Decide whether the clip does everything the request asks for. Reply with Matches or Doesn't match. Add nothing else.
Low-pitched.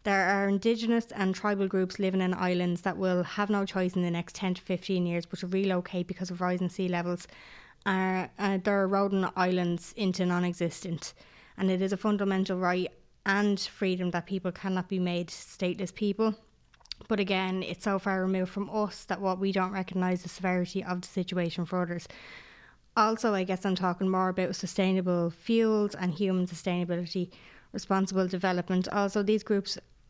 Doesn't match